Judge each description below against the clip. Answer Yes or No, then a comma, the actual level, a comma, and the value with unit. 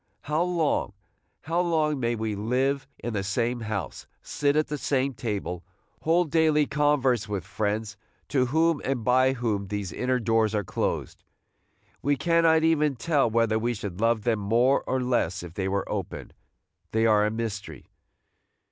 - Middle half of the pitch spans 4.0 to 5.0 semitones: No, wide, 5.4 semitones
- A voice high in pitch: No, low, 120 Hz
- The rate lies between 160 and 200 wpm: Yes, average, 165 wpm